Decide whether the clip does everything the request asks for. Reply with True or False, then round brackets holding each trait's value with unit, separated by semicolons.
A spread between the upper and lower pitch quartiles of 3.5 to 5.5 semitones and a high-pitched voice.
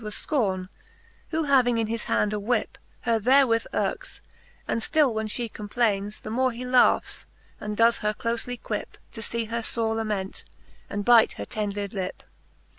False (2.6 semitones; 225 Hz)